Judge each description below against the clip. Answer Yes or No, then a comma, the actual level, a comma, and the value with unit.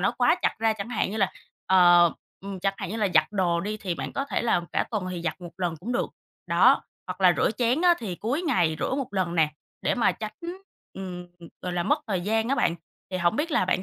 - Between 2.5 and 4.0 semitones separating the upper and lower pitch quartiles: No, average, 4.4 semitones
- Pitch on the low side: No, high, 195 Hz